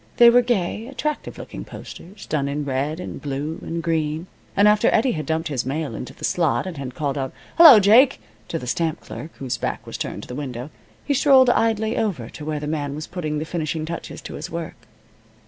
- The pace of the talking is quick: Yes, fast, 215 wpm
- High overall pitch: No, medium, 160 Hz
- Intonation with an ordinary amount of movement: No, wide, 6.5 semitones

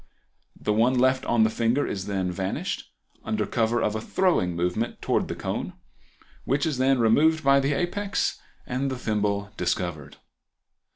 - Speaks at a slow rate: No, average, 160 wpm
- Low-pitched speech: Yes, low, 115 Hz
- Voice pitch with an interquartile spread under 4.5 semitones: No, average, 5.1 semitones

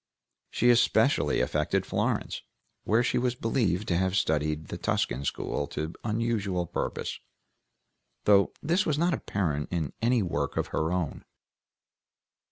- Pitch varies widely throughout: Yes, wide, 6.8 semitones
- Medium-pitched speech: No, very low, 95 Hz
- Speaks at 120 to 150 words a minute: Yes, slow, 135 wpm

